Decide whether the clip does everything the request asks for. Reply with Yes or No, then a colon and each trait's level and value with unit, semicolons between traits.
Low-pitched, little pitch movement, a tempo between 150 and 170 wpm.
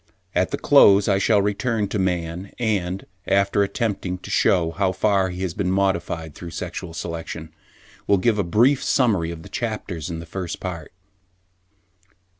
No: very low, 95 Hz; average, 3.0 semitones; average, 165 wpm